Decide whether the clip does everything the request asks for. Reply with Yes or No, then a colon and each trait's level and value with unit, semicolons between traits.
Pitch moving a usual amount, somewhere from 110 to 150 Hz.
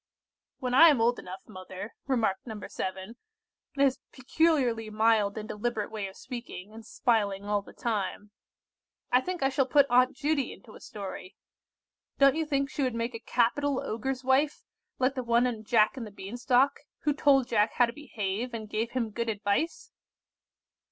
No: average, 4.0 semitones; high, 235 Hz